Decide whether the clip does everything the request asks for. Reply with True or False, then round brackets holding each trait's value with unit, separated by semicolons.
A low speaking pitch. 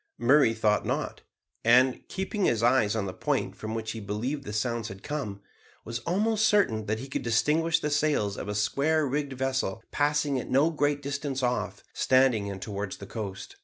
True (125 Hz)